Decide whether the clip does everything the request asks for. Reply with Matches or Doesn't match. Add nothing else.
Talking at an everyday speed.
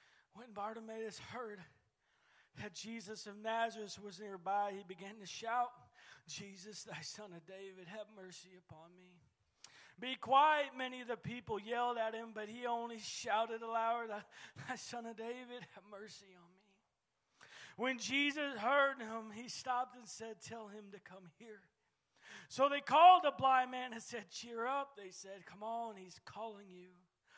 Matches